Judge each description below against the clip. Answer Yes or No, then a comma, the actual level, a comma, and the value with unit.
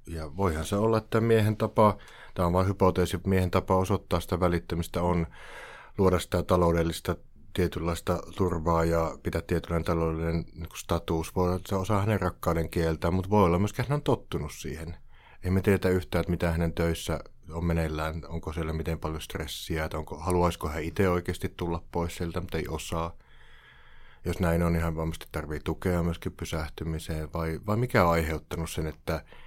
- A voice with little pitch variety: Yes, narrow, 2.2 semitones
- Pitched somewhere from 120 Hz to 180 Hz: No, very low, 85 Hz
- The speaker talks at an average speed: No, fast, 175 wpm